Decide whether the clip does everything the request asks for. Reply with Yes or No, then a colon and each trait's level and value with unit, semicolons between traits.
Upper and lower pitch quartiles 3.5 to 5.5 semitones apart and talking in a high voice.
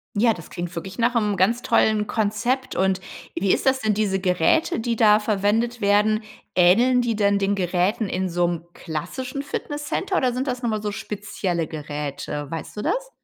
Yes: average, 4.5 semitones; high, 210 Hz